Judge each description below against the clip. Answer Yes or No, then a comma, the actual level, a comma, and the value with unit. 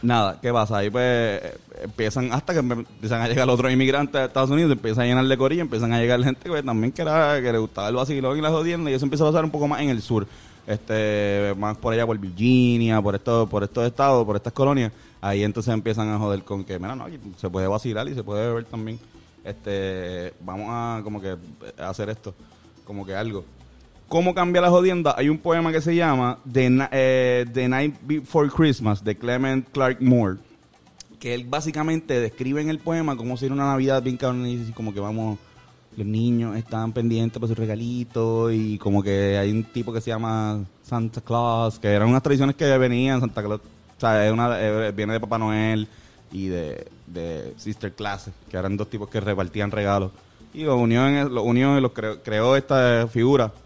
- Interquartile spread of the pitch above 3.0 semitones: Yes, average, 3.8 semitones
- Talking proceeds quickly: Yes, fast, 210 wpm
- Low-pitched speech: Yes, low, 115 Hz